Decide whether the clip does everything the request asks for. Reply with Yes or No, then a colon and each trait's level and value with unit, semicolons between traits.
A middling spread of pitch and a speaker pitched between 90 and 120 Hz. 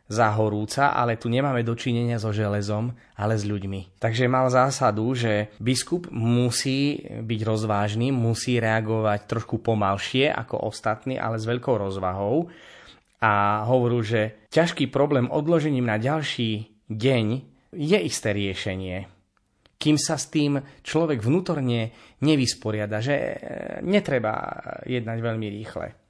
Yes: average, 4.0 semitones; low, 115 Hz